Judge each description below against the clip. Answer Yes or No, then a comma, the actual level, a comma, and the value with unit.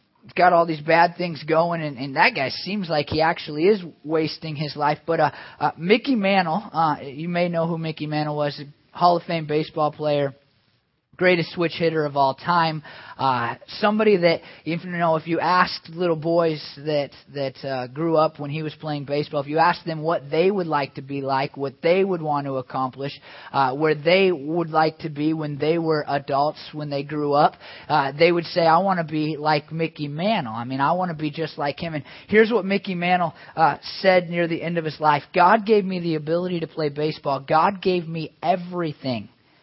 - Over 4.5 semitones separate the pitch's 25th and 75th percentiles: No, average, 2.8 semitones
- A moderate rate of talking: No, fast, 210 wpm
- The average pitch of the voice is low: No, medium, 155 Hz